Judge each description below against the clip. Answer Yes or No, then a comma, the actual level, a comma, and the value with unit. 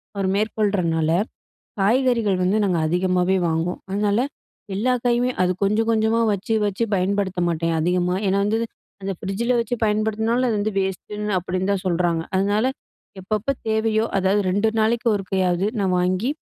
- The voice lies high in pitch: Yes, high, 200 Hz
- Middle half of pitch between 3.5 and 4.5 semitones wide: No, average, 3.1 semitones